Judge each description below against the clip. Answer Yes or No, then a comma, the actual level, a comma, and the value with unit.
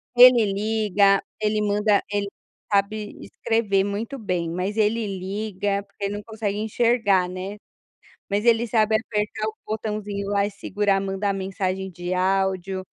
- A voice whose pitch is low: No, high, 205 Hz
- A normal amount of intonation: No, narrow, 1.8 semitones